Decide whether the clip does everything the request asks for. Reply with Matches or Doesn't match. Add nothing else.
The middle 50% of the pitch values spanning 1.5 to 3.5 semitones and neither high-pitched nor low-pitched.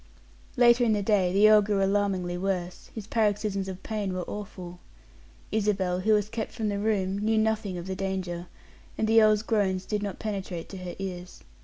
Doesn't match